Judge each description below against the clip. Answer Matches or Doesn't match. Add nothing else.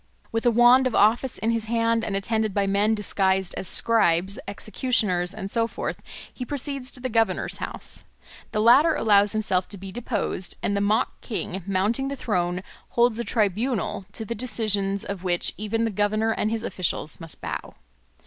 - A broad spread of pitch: Doesn't match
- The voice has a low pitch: Doesn't match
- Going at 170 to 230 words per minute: Matches